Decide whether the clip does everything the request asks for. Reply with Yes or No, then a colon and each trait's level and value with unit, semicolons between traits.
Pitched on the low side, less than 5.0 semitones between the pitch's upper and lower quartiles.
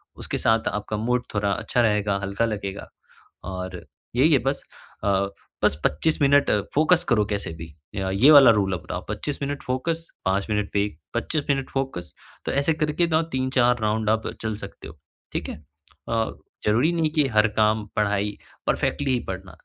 No: low, 110 Hz; average, 5.3 semitones